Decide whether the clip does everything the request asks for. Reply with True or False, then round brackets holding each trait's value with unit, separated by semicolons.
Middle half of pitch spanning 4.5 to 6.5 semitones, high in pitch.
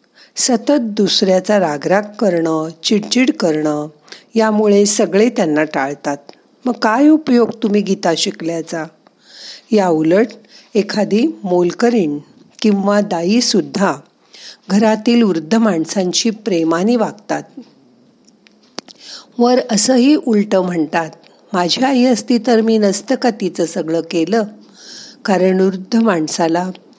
True (5.0 semitones; 205 Hz)